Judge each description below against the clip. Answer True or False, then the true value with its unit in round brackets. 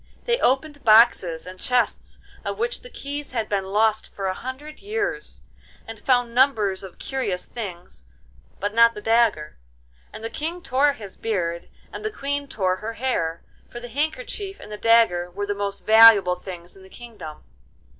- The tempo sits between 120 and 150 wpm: False (175 wpm)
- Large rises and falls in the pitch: True (6.0 semitones)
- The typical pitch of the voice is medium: False (225 Hz)